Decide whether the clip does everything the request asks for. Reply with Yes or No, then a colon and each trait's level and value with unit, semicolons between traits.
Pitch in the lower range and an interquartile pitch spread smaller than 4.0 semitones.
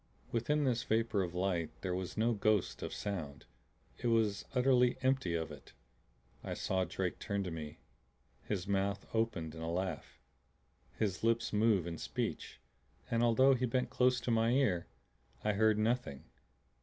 No: low, 105 Hz; average, 4.4 semitones